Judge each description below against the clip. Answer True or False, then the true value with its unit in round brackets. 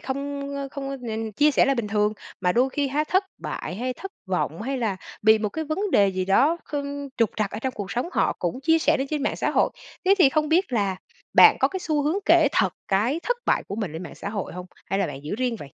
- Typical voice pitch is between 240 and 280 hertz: True (255 Hz)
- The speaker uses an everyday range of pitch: False (6.5 semitones)